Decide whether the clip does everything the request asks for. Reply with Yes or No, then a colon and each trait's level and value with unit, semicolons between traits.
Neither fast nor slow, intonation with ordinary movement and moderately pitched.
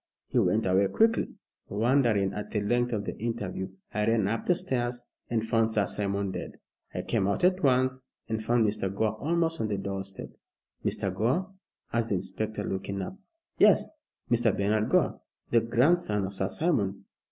No: average, 175 wpm; average, 3.5 semitones; low, 110 Hz